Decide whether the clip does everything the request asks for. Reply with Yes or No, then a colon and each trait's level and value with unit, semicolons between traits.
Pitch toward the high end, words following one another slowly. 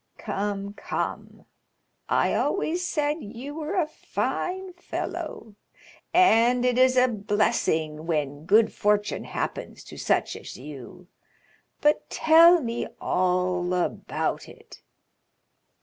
Yes: high, 225 Hz; slow, 110 wpm